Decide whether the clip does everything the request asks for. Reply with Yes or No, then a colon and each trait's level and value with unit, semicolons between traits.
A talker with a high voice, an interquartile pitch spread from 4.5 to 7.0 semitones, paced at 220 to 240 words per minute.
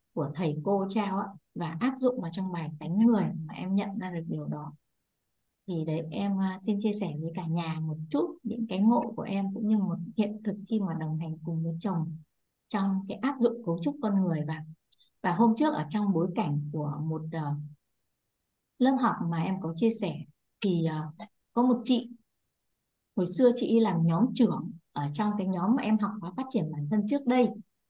No: high, 195 Hz; wide, 5.4 semitones; average, 205 wpm